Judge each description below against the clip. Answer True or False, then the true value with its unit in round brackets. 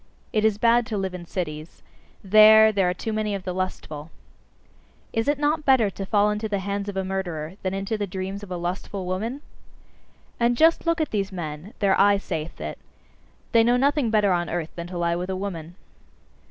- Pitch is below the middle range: False (195 Hz)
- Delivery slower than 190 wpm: False (205 wpm)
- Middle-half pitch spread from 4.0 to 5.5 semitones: False (3.3 semitones)